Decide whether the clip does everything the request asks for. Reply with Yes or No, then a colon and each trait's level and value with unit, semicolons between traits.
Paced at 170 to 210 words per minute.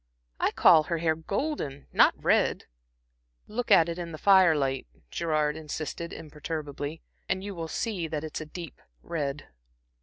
No: average, 155 wpm